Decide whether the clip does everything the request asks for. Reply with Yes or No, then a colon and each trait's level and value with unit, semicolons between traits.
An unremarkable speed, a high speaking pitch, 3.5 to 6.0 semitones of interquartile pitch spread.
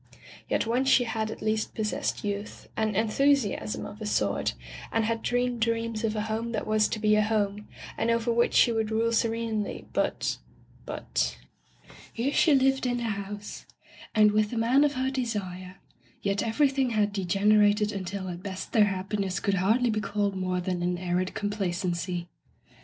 No: average, 180 wpm; high, 215 Hz; average, 2.7 semitones